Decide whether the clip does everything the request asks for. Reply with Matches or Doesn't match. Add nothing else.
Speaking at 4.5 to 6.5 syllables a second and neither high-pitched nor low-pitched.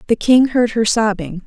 Doesn't match